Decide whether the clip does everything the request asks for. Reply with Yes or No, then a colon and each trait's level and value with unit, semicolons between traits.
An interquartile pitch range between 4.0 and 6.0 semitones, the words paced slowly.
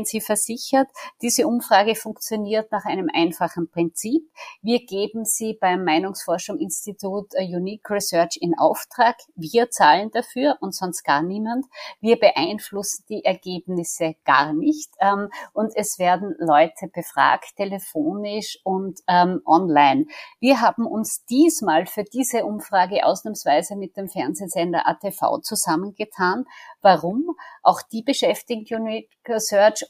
Yes: average, 4.4 semitones; slow, 120 wpm